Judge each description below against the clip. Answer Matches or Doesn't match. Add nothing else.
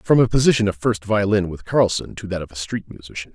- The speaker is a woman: Doesn't match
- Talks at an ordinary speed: Doesn't match